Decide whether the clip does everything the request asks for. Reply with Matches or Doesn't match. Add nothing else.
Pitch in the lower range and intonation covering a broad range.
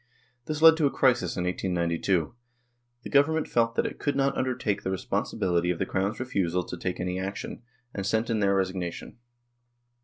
Matches